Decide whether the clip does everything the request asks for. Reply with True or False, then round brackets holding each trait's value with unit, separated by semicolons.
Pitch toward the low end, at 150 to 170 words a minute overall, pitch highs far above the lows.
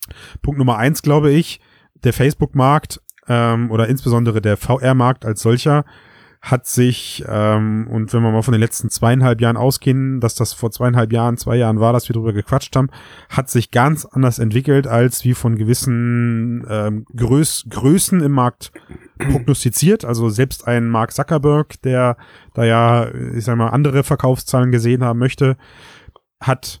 False (120 Hz; 160 wpm; 2.4 semitones)